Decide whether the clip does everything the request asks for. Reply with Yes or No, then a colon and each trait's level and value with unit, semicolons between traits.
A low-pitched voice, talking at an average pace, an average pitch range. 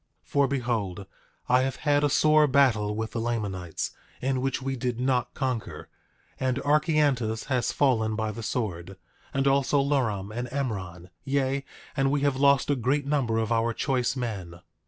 Yes: low, 125 Hz; average, 170 wpm; average, 3.9 semitones